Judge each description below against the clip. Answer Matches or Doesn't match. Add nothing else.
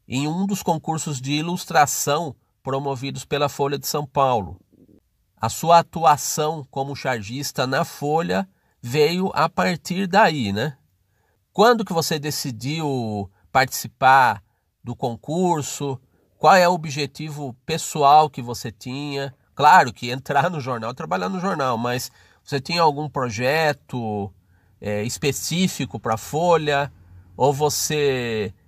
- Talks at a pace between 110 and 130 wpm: Matches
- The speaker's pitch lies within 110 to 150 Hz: Matches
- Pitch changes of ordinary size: Matches